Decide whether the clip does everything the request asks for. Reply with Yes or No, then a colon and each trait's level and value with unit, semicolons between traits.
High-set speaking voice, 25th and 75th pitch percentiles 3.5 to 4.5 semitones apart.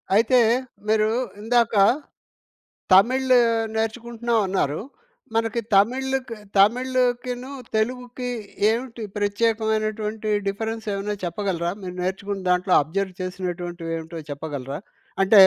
Yes: high, 215 Hz; average, 4.0 semitones